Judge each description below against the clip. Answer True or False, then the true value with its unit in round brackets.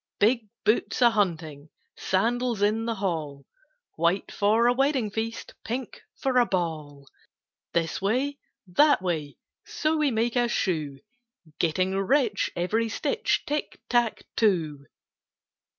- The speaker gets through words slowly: True (125 wpm)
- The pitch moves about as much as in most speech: False (6.1 semitones)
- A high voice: True (210 Hz)